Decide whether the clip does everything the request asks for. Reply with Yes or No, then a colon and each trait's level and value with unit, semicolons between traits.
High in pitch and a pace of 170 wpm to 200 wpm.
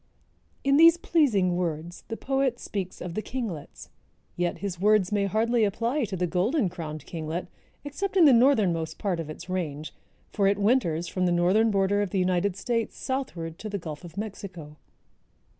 Yes: high, 195 Hz; average, 175 wpm